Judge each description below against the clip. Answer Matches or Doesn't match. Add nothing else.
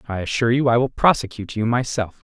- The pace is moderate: Doesn't match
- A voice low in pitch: Matches